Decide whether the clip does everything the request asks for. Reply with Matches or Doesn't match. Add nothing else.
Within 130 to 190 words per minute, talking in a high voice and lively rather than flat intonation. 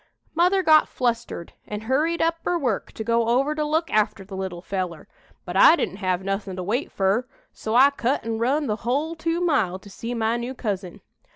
Doesn't match